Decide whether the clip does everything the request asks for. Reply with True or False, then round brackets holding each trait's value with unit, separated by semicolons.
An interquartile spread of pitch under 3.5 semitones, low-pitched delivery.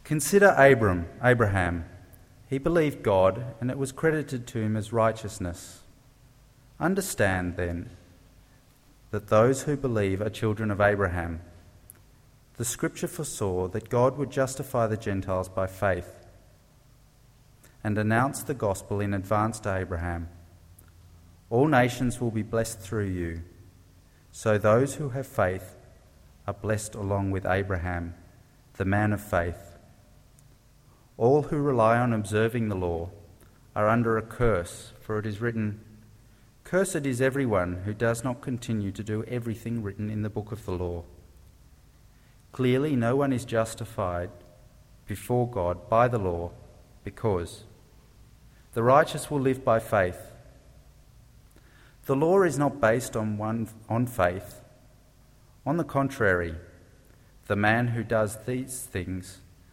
False (5.0 semitones; 110 Hz)